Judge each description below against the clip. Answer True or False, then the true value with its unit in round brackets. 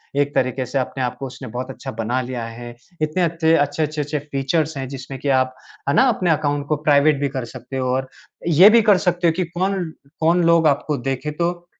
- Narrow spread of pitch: False (4.1 semitones)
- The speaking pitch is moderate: True (145 Hz)